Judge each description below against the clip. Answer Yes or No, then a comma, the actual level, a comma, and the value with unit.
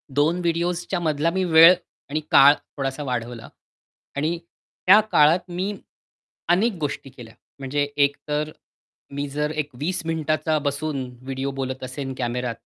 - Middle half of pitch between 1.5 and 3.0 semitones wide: No, average, 3.5 semitones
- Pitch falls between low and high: Yes, medium, 150 Hz